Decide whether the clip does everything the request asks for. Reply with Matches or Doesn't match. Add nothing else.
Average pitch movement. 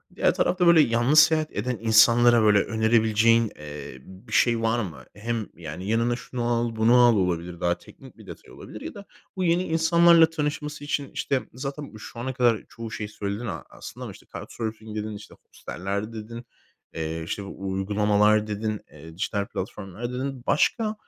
Matches